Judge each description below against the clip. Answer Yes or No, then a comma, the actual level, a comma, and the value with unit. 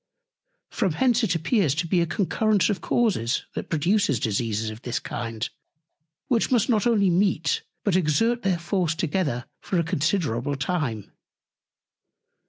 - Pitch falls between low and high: Yes, medium, 170 Hz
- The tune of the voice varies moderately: No, wide, 6.4 semitones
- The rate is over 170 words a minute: No, average, 145 wpm